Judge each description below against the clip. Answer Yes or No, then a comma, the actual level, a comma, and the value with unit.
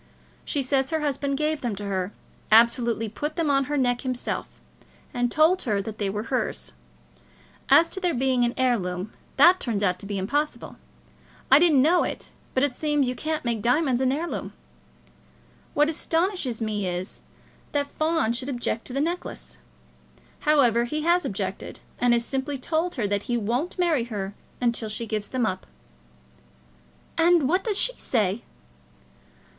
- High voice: Yes, very high, 255 Hz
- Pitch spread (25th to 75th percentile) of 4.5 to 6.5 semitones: Yes, average, 5.2 semitones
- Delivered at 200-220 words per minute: No, average, 165 wpm